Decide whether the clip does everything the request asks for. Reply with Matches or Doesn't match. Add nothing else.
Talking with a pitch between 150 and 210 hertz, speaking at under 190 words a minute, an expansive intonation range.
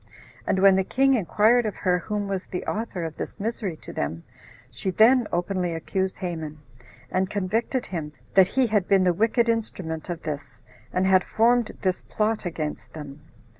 Doesn't match